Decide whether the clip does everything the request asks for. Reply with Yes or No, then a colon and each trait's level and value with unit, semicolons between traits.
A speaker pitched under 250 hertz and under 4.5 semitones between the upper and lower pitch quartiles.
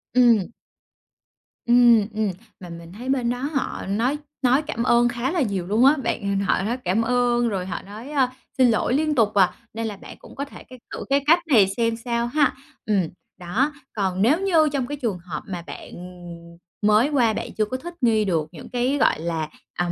No: high, 230 Hz; average, 4.8 semitones